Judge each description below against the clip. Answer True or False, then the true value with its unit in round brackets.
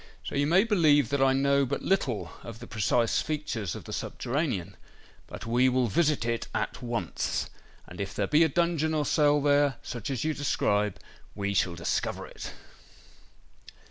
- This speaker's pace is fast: False (175 wpm)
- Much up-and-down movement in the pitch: False (4.7 semitones)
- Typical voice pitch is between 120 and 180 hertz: True (135 Hz)